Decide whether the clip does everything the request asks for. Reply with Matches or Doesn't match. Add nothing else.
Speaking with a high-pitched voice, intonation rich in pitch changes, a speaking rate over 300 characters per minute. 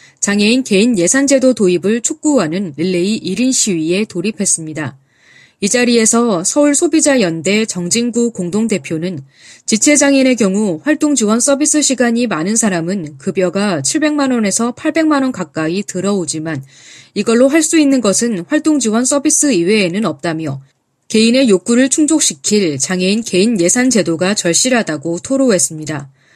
Matches